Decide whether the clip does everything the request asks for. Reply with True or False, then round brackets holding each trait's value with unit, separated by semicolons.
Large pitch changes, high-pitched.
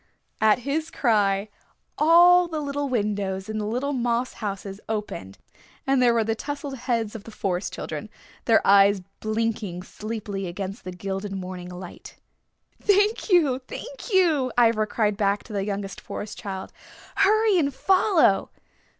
True (6.0 semitones; 220 Hz)